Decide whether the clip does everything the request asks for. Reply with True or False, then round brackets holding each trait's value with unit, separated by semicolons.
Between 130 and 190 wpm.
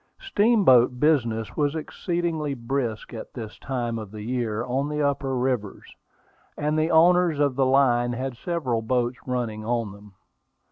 True (150 wpm)